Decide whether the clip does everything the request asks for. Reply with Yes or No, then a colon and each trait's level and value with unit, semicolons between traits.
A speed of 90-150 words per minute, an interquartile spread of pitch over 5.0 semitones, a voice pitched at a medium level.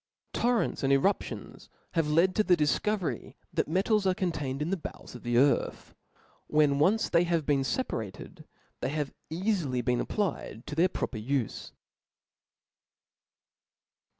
Yes: average, 145 wpm; wide, 5.4 semitones; medium, 155 Hz